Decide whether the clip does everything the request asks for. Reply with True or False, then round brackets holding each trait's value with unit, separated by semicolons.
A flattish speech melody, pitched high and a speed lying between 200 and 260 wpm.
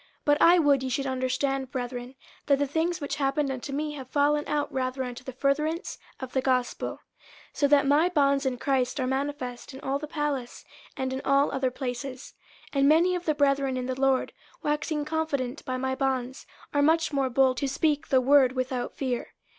True (2.1 semitones; 275 Hz; 205 wpm)